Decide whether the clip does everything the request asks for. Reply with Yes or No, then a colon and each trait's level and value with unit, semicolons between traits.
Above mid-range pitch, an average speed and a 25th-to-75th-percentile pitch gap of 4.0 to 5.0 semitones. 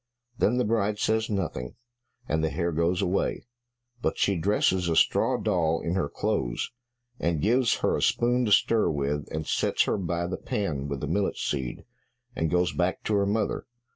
No: very low, 90 Hz; average, 185 wpm; average, 4.6 semitones